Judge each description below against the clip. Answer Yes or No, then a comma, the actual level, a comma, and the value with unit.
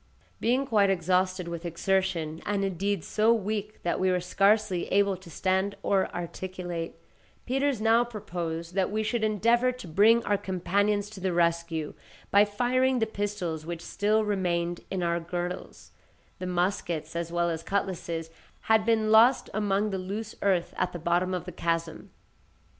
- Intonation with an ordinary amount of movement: Yes, average, 3.5 semitones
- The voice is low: No, high, 190 Hz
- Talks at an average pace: Yes, average, 160 wpm